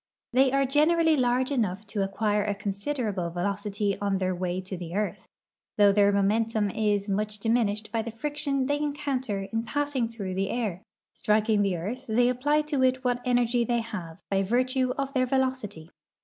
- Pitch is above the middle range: Yes, high, 220 Hz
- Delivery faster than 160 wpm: Yes, average, 175 wpm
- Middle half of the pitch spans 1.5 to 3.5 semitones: No, average, 4.4 semitones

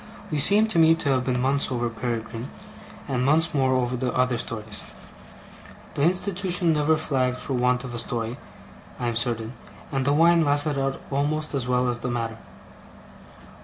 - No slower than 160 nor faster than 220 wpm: Yes, average, 175 wpm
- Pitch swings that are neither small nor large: Yes, average, 3.7 semitones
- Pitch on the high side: No, low, 130 Hz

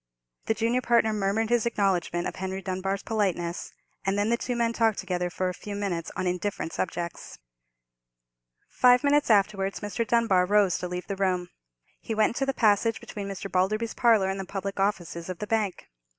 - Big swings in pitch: No, average, 3.3 semitones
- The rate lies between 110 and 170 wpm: No, average, 185 wpm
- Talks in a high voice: Yes, high, 200 Hz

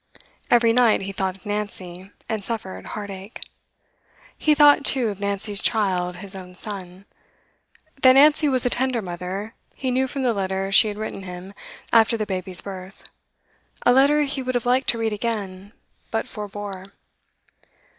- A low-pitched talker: No, high, 205 Hz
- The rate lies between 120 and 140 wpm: No, average, 160 wpm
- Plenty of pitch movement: No, average, 4.3 semitones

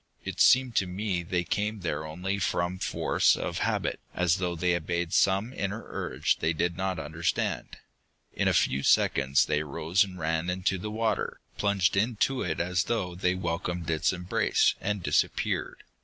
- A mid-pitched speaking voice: No, very low, 90 Hz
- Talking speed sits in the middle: Yes, average, 170 wpm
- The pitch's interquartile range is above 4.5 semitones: No, average, 2.7 semitones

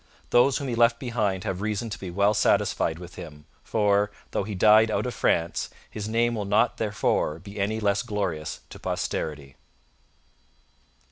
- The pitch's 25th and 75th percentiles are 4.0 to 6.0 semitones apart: No, average, 3.1 semitones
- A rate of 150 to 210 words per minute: Yes, average, 165 wpm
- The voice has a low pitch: Yes, low, 105 Hz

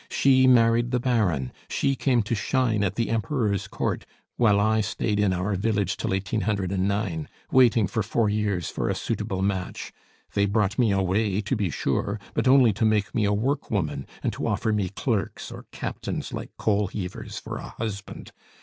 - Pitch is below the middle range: Yes, low, 105 Hz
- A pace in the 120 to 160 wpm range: No, average, 175 wpm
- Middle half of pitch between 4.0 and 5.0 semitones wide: No, average, 2.8 semitones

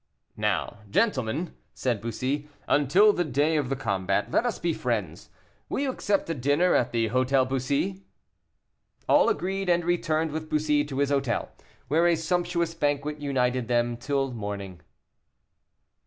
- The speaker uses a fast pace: No, average, 150 wpm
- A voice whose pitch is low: No, medium, 145 Hz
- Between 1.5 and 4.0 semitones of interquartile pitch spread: No, average, 5.1 semitones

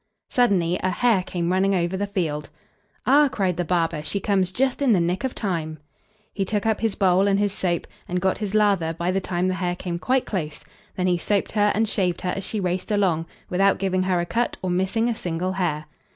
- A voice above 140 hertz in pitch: Yes, medium, 185 Hz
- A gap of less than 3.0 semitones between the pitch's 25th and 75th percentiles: Yes, narrow, 2.6 semitones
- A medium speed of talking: No, fast, 225 wpm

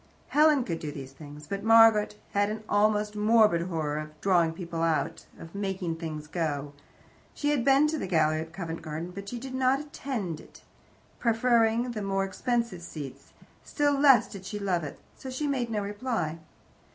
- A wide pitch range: Yes, wide, 6.4 semitones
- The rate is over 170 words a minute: Yes, average, 180 wpm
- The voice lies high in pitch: Yes, high, 200 Hz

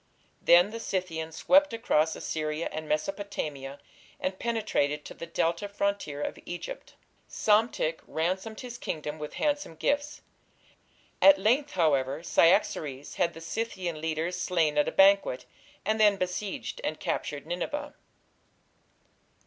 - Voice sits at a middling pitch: Yes, medium, 180 Hz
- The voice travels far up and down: Yes, wide, 5.8 semitones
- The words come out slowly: Yes, slow, 125 wpm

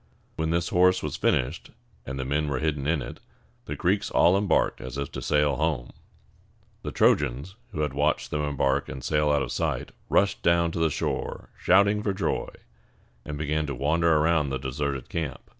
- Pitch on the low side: Yes, very low, 75 Hz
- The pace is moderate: Yes, average, 190 wpm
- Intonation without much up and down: No, average, 3.1 semitones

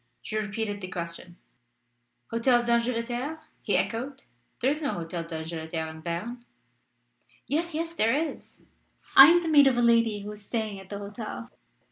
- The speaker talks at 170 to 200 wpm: No, average, 160 wpm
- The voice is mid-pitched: No, high, 230 Hz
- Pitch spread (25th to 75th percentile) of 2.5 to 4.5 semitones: No, average, 5.2 semitones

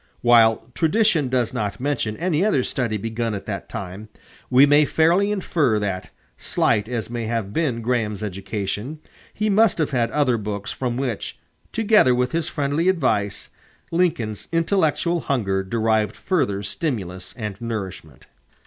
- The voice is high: No, low, 120 Hz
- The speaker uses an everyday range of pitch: No, wide, 6.7 semitones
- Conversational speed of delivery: Yes, average, 145 wpm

